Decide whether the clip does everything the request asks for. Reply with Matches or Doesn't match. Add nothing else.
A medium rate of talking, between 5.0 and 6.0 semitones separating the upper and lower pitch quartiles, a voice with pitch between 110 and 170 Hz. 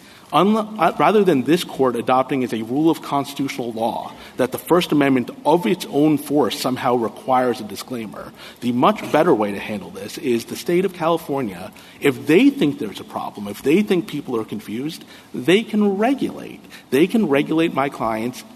Matches